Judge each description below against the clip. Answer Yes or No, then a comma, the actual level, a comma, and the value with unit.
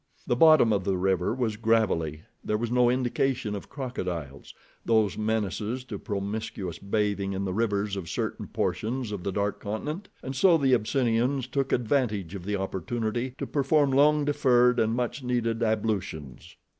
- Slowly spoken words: No, average, 160 wpm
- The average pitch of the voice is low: Yes, low, 110 Hz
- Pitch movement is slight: No, average, 4.2 semitones